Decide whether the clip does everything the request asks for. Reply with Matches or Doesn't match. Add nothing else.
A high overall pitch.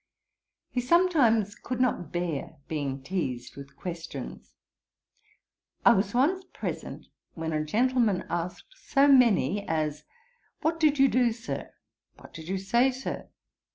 Matches